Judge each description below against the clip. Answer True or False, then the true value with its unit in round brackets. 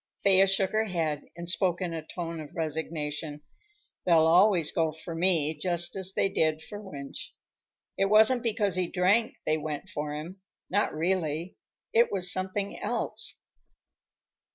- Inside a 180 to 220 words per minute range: False (155 wpm)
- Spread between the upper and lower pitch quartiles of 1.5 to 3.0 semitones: False (3.5 semitones)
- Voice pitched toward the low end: False (175 Hz)